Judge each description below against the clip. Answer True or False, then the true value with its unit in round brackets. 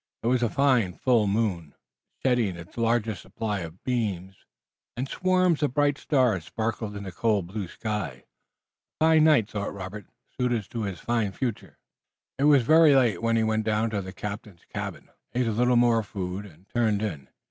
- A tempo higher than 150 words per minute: True (180 wpm)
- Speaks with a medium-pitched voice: False (110 Hz)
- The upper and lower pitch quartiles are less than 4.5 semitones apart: True (3.7 semitones)